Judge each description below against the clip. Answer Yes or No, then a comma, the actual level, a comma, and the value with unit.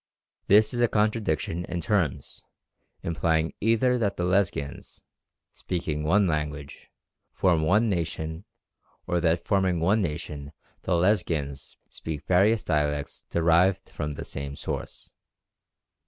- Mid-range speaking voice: No, very low, 85 Hz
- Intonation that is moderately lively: Yes, average, 4.4 semitones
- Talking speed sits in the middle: No, slow, 120 wpm